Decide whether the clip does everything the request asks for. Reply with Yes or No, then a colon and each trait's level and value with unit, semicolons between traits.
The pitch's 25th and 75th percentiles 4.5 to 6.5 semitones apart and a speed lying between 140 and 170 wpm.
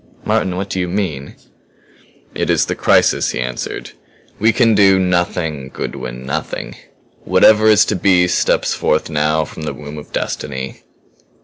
Yes: average, 4.9 semitones; average, 150 wpm